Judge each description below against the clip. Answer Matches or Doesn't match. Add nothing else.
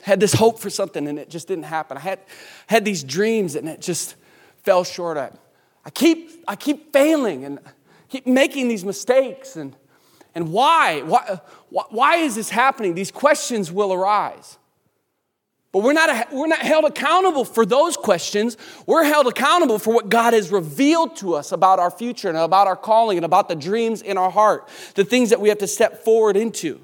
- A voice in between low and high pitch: Doesn't match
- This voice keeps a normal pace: Matches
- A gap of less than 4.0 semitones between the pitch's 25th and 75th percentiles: Doesn't match